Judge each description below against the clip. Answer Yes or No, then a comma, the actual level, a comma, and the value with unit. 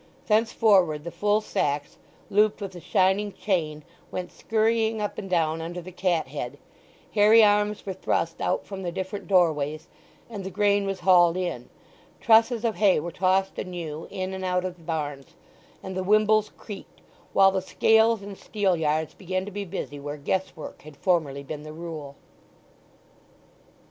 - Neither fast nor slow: Yes, average, 170 wpm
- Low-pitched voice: No, medium, 185 Hz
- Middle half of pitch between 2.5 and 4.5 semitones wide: Yes, average, 4.2 semitones